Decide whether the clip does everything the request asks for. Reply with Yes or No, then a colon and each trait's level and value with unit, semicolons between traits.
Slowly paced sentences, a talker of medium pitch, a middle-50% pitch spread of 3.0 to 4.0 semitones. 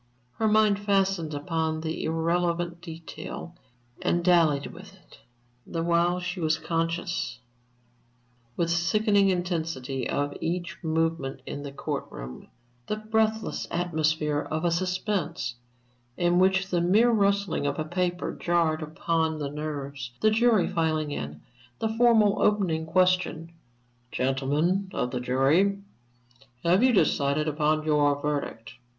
Yes: slow, 130 wpm; medium, 170 Hz; average, 3.6 semitones